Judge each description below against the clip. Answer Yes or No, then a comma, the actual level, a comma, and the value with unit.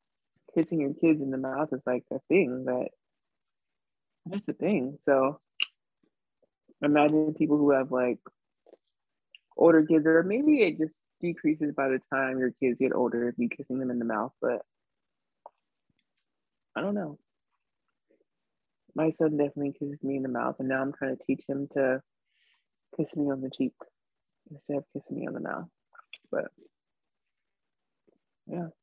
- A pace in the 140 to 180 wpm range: Yes, average, 155 wpm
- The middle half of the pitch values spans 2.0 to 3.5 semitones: Yes, average, 2.9 semitones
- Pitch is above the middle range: No, medium, 140 Hz